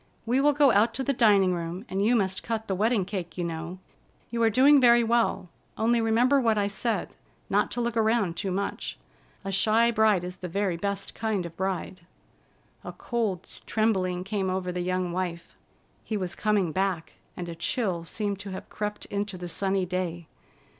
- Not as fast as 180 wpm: No, average, 190 wpm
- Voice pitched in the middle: No, high, 200 Hz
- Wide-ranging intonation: No, average, 3.7 semitones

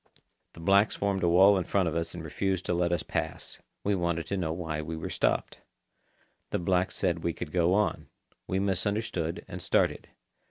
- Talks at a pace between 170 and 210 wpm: Yes, average, 195 wpm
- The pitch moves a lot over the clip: No, narrow, 2.6 semitones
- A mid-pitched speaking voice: No, very low, 90 Hz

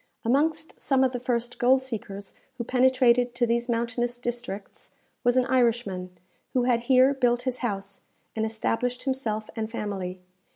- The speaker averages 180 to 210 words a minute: No, average, 155 wpm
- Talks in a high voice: Yes, high, 240 Hz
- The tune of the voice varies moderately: No, narrow, 2.3 semitones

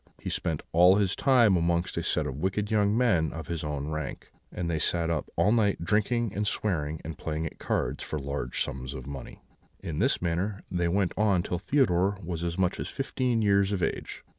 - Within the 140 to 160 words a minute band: No, fast, 205 wpm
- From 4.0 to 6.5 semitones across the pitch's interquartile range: Yes, average, 4.4 semitones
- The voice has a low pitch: Yes, very low, 90 Hz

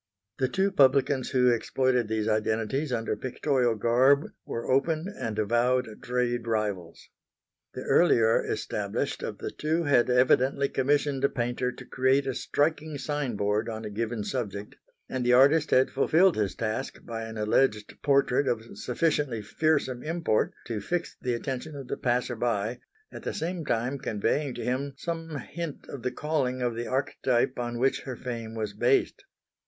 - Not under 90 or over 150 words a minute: No, average, 165 wpm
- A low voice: Yes, low, 125 Hz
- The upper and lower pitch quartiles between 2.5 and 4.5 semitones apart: Yes, average, 3.5 semitones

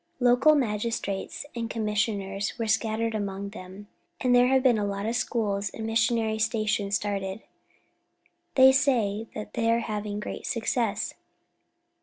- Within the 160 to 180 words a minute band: No, average, 145 wpm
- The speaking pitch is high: Yes, high, 220 Hz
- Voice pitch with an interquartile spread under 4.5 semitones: Yes, narrow, 2.4 semitones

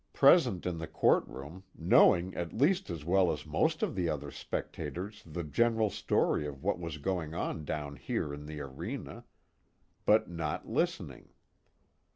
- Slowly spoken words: No, average, 155 wpm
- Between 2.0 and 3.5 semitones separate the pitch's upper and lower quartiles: No, average, 4.3 semitones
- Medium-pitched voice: No, very low, 85 Hz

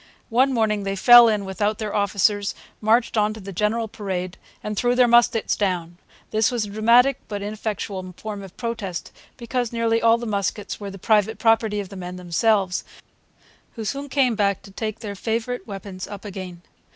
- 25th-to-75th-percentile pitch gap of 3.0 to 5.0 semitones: No, narrow, 2.6 semitones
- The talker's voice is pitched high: Yes, high, 210 Hz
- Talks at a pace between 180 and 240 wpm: Yes, average, 185 wpm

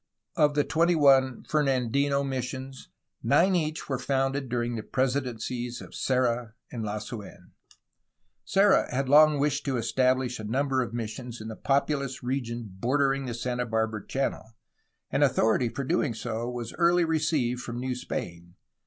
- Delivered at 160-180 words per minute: No, average, 150 wpm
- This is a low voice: Yes, low, 130 Hz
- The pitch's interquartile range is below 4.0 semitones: Yes, average, 2.9 semitones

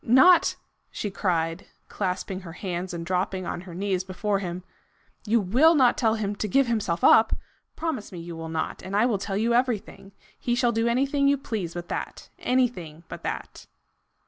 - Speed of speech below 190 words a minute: No, average, 195 wpm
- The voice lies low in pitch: No, high, 200 Hz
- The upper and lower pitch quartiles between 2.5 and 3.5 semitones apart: No, average, 4.9 semitones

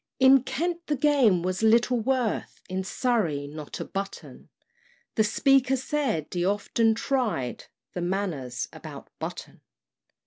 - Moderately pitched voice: No, high, 220 Hz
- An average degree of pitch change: No, wide, 6.4 semitones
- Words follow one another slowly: Yes, slow, 130 wpm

